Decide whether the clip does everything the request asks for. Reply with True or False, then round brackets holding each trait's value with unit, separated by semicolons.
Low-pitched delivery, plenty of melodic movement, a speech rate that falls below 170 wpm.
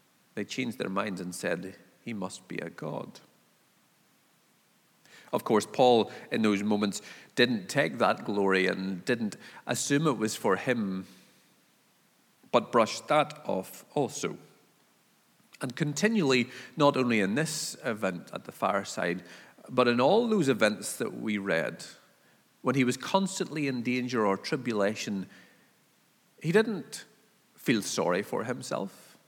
True (120 Hz; 6.5 semitones; 135 wpm)